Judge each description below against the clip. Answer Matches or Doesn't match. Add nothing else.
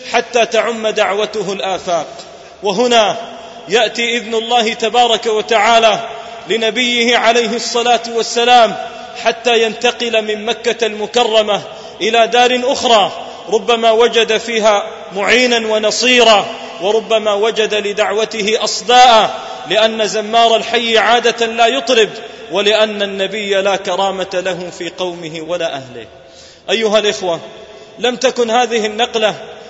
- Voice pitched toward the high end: Matches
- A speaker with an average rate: Matches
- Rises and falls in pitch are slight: Matches